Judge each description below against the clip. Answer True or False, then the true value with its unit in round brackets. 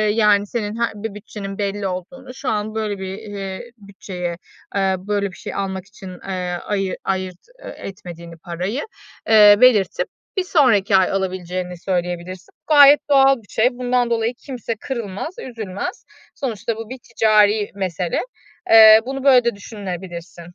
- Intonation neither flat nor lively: True (3.6 semitones)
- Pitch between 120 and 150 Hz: False (205 Hz)